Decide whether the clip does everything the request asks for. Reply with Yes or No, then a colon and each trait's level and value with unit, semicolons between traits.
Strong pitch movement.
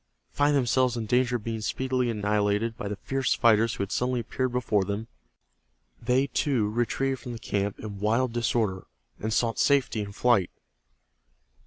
No: average, 3.1 semitones